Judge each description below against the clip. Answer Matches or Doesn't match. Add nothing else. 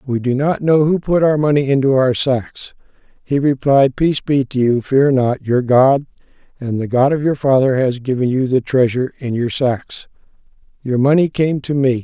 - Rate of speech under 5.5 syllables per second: Matches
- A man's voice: Matches